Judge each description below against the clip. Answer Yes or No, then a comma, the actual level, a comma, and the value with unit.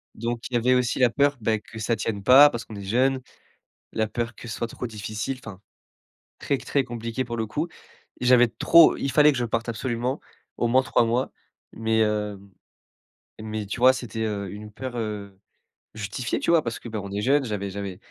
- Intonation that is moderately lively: Yes, average, 3.0 semitones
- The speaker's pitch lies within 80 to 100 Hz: No, low, 115 Hz